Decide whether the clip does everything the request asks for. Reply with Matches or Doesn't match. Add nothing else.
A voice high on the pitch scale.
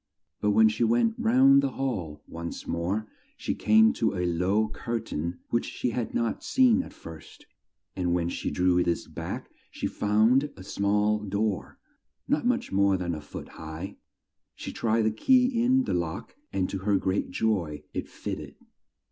Doesn't match